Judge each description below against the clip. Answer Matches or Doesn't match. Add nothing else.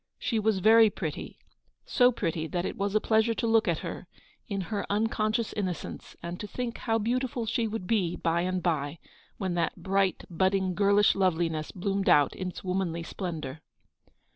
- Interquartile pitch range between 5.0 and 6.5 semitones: Doesn't match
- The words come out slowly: Doesn't match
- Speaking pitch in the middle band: Doesn't match